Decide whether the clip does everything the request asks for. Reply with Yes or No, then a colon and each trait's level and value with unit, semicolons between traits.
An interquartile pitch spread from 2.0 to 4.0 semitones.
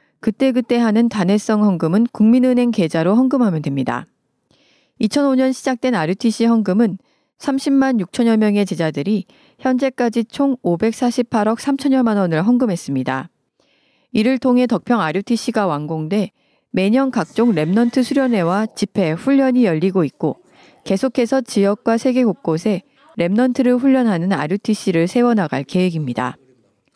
No: wide, 5.4 semitones